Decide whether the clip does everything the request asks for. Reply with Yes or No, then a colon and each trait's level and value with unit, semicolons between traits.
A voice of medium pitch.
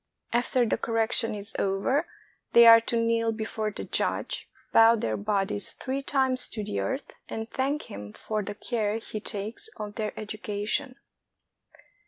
No: high, 225 Hz